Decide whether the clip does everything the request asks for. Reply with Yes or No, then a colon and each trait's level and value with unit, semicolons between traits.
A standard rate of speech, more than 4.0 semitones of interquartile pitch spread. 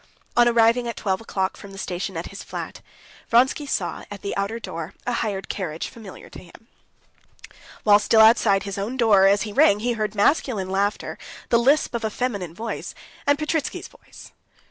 No: average, 185 wpm; average, 3.2 semitones